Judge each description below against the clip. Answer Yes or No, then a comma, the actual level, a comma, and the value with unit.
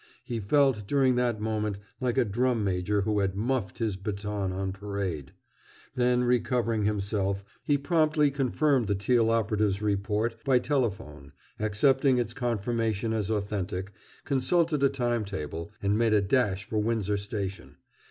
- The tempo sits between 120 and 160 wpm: Yes, average, 145 wpm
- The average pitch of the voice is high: No, low, 110 Hz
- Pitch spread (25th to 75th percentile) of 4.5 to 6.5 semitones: No, average, 3.8 semitones